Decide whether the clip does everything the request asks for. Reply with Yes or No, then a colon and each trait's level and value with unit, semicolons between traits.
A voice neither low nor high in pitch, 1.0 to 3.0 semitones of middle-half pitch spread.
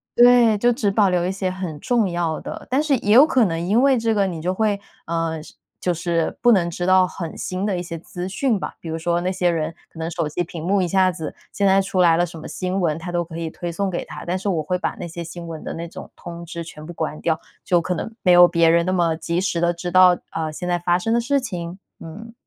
Yes: medium, 175 Hz; narrow, 2.6 semitones